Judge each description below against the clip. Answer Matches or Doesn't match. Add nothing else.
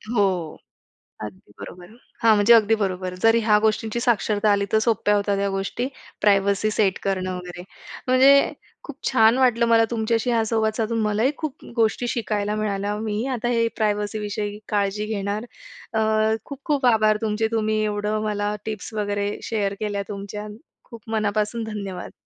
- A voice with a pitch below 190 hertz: Doesn't match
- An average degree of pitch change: Doesn't match